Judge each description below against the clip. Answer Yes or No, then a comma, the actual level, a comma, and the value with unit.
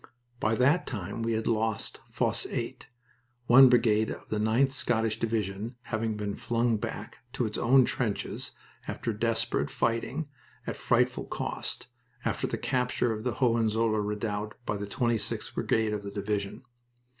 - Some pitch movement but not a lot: No, narrow, 2.1 semitones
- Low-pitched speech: Yes, low, 110 Hz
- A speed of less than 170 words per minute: Yes, average, 150 wpm